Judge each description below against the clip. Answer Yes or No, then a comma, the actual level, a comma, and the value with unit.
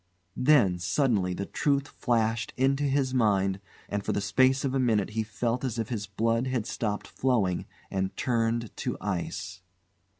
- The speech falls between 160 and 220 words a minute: Yes, average, 165 wpm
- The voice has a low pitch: Yes, low, 115 Hz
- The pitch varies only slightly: No, average, 4.4 semitones